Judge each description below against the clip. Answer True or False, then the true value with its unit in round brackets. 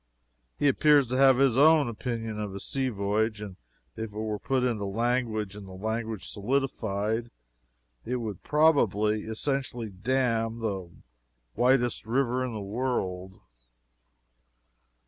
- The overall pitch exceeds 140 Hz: False (115 Hz)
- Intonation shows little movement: False (3.6 semitones)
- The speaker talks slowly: True (130 wpm)